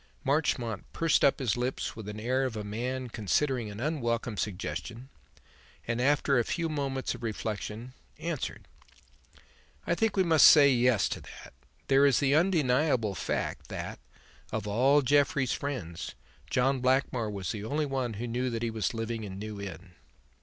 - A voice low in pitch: Yes, low, 125 Hz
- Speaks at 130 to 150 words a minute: No, average, 165 wpm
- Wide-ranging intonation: No, average, 4.1 semitones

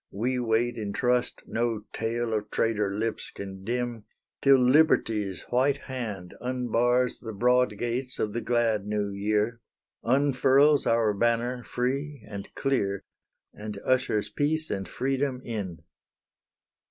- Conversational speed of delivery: No, slow, 130 wpm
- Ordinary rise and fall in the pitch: Yes, average, 3.2 semitones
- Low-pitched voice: Yes, low, 120 Hz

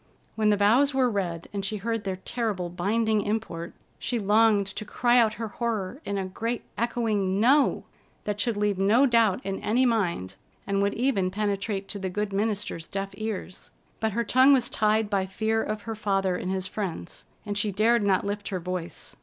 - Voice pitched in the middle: No, high, 205 Hz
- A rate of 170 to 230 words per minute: Yes, average, 195 wpm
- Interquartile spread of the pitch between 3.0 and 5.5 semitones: No, narrow, 2.6 semitones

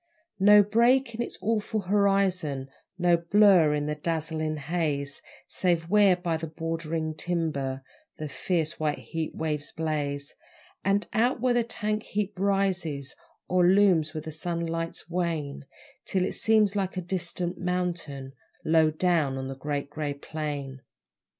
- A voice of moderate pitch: Yes, medium, 165 Hz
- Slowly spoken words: No, average, 145 wpm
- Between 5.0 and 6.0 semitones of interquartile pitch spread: No, average, 4.2 semitones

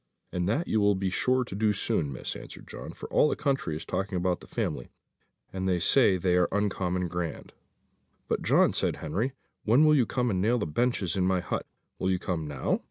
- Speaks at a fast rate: Yes, fast, 220 wpm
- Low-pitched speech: Yes, very low, 95 Hz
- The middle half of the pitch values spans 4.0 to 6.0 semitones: Yes, average, 4.6 semitones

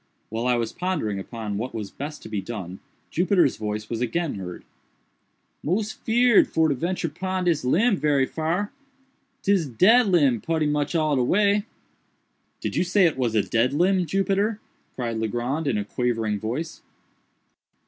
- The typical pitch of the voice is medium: Yes, medium, 150 Hz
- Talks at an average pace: Yes, average, 160 wpm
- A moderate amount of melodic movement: No, wide, 8.3 semitones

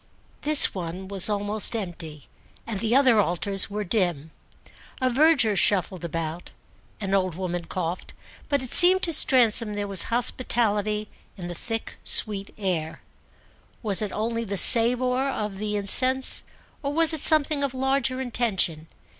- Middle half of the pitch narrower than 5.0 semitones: No, average, 5.3 semitones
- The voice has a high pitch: Yes, high, 210 Hz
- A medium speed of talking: Yes, average, 145 wpm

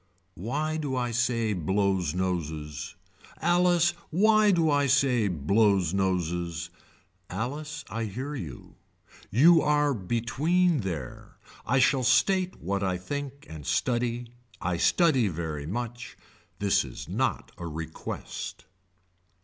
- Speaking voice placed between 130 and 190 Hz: No, low, 115 Hz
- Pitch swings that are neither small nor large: No, wide, 8.4 semitones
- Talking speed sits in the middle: No, slow, 115 wpm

